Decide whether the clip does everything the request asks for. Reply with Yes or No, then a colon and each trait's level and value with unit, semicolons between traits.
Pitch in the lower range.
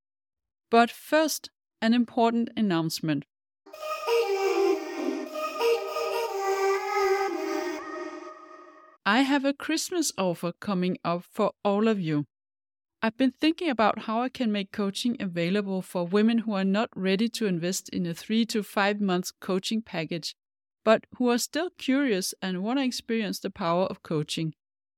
No: high, 225 Hz